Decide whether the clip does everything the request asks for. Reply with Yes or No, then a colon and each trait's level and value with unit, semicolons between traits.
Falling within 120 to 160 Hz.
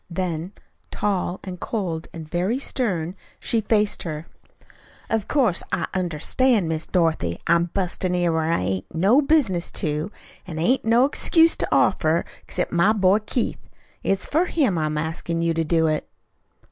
No: medium, 180 Hz